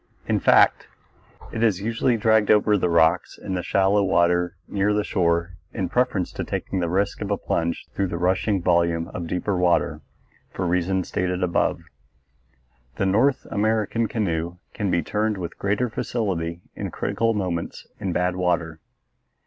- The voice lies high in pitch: No, very low, 95 Hz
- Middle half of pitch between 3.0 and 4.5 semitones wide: Yes, average, 3.3 semitones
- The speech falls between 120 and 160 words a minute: Yes, average, 155 wpm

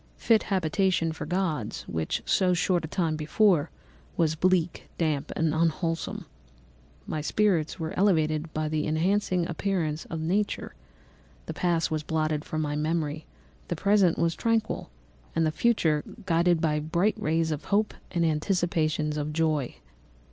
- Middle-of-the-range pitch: Yes, medium, 165 Hz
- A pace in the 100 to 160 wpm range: Yes, average, 145 wpm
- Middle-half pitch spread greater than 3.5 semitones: No, average, 2.8 semitones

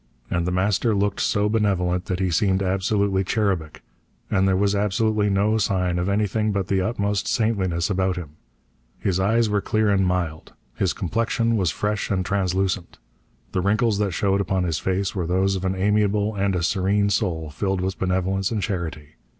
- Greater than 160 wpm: Yes, average, 180 wpm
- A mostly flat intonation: Yes, narrow, 2.1 semitones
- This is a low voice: Yes, very low, 95 Hz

